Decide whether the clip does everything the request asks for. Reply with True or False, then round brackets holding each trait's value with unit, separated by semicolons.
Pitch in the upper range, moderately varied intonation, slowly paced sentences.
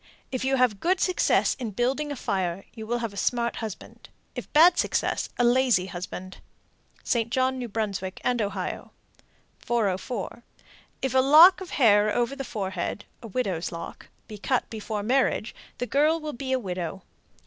False (235 Hz; 4.6 semitones; 160 wpm)